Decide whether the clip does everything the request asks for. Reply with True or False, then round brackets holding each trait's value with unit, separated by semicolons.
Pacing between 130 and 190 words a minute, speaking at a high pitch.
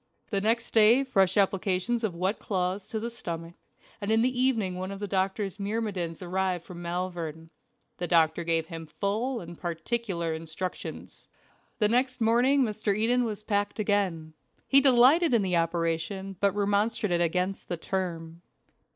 True (155 wpm; 195 Hz)